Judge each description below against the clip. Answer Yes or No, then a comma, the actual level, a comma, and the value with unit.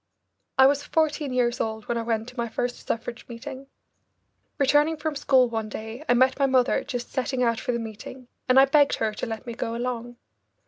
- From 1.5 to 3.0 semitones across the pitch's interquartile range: Yes, average, 2.7 semitones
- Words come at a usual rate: No, fast, 210 wpm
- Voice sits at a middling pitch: No, high, 245 Hz